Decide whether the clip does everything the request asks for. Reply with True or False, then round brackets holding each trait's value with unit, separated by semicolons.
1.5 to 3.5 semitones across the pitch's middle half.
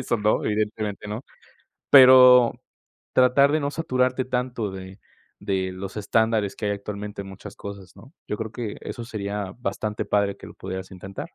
False (3.9 semitones)